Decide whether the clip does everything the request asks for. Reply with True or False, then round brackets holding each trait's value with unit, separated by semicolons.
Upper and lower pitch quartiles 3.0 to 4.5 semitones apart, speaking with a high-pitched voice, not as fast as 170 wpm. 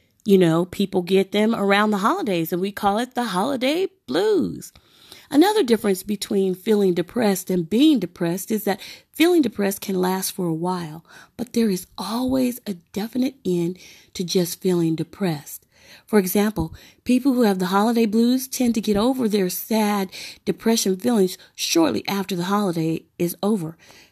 True (3.9 semitones; 200 Hz; 160 wpm)